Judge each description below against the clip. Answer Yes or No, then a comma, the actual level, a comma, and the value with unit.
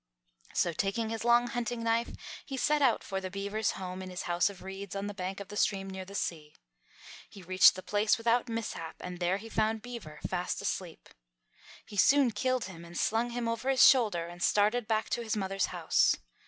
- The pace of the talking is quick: Yes, fast, 210 wpm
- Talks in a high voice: Yes, high, 205 Hz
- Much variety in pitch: No, average, 3.7 semitones